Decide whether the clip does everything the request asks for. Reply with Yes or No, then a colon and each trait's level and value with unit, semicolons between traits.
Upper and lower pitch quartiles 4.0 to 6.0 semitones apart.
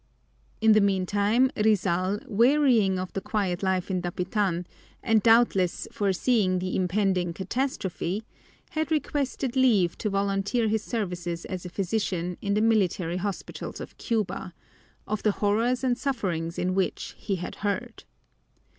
No: average, 3.5 semitones